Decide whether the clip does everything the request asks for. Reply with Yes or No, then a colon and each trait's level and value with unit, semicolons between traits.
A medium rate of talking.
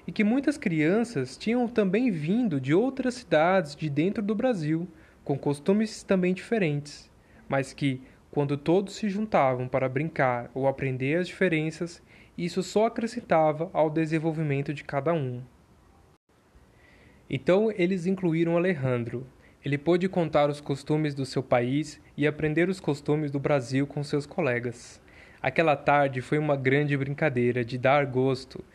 Yes: average, 140 wpm